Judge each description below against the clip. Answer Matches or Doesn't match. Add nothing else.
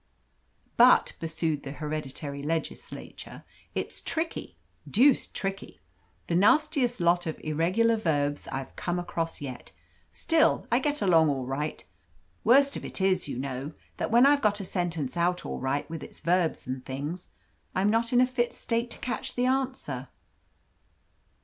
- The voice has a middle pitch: Matches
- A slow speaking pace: Doesn't match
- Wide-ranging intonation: Matches